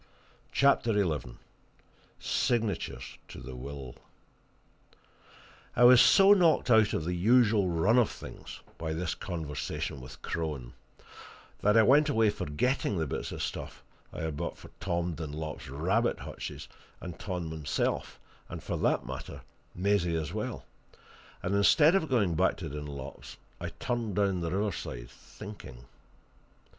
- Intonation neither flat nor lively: No, wide, 6.4 semitones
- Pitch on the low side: Yes, very low, 90 Hz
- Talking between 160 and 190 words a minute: No, average, 140 wpm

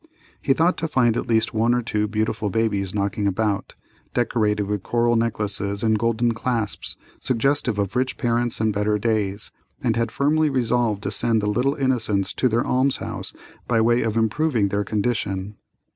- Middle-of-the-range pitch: No, low, 110 Hz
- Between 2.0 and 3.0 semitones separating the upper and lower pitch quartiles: Yes, average, 2.7 semitones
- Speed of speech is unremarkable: Yes, average, 175 wpm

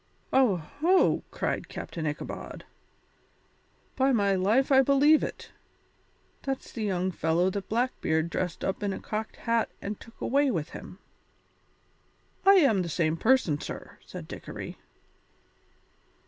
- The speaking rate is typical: No, slow, 130 wpm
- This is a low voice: No, high, 210 Hz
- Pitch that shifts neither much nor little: No, wide, 6.9 semitones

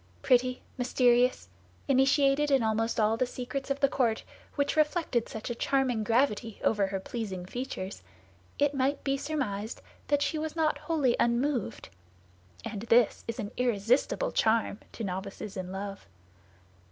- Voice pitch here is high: Yes, high, 245 Hz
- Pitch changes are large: No, average, 4.2 semitones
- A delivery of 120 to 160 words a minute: Yes, average, 145 wpm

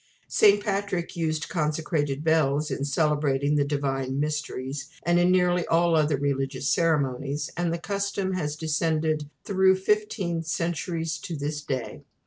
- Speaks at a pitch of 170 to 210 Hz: No, medium, 155 Hz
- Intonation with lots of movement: No, average, 3.2 semitones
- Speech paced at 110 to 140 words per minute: Yes, slow, 135 wpm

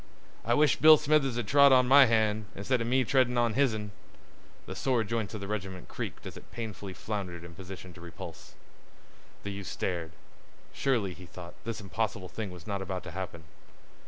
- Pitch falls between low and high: No, low, 105 Hz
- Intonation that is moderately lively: Yes, average, 4.8 semitones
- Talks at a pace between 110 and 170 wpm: No, average, 185 wpm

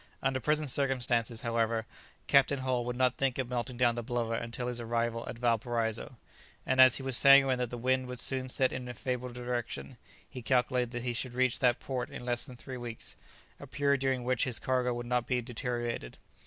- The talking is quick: Yes, fast, 210 wpm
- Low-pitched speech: Yes, low, 125 Hz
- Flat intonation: Yes, narrow, 1.5 semitones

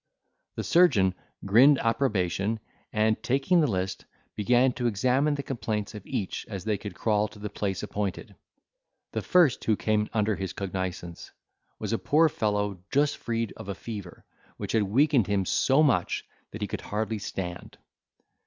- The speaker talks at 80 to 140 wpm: No, average, 165 wpm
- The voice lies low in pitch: Yes, low, 110 Hz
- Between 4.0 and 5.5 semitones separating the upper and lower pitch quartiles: Yes, average, 4.3 semitones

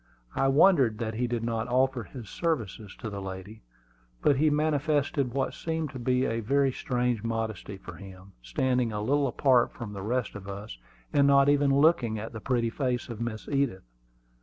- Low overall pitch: Yes, low, 120 Hz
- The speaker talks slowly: No, average, 185 wpm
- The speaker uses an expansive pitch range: No, average, 4.1 semitones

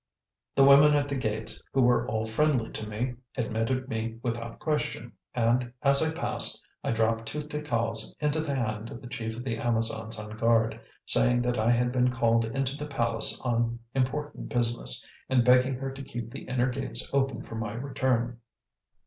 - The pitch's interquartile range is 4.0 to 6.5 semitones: No, average, 2.9 semitones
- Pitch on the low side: Yes, low, 120 Hz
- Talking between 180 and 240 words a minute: Yes, average, 185 wpm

